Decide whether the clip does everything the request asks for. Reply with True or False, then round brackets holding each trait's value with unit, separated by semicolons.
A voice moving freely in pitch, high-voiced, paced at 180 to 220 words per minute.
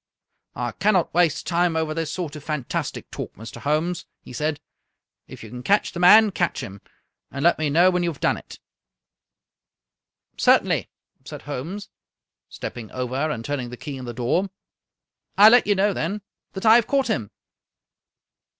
False (5.9 semitones; 160 Hz; 185 wpm)